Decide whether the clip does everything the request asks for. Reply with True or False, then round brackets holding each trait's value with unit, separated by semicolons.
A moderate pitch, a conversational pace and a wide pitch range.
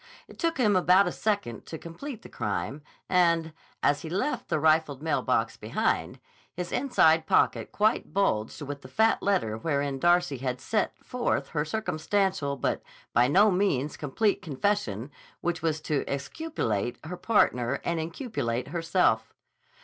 True (160 Hz; 150 wpm; 6.2 semitones)